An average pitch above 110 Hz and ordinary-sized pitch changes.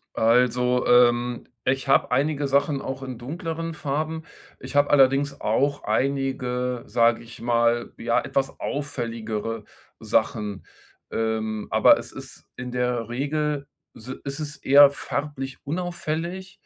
Yes: low, 135 Hz; average, 3.2 semitones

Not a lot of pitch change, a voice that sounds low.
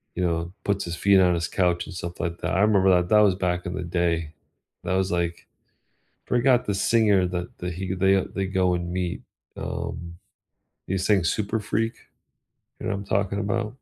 Yes: narrow, 2.3 semitones; very low, 95 Hz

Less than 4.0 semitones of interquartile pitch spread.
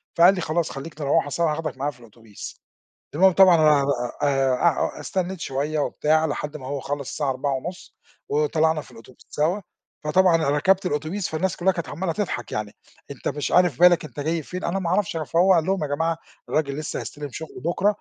Yes: average, 3.6 semitones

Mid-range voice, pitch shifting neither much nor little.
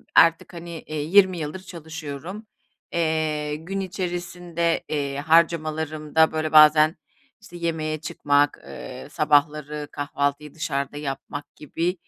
No: medium, 155 Hz; narrow, 2.2 semitones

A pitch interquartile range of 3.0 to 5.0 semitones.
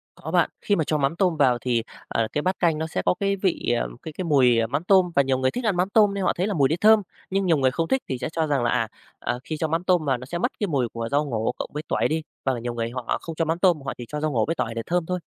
No: wide, 5.6 semitones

